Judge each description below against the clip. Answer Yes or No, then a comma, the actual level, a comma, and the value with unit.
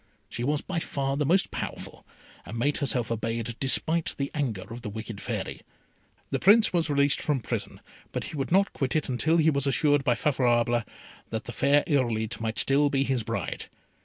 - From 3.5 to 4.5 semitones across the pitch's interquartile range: Yes, average, 3.9 semitones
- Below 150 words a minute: No, average, 190 wpm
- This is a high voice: No, low, 135 Hz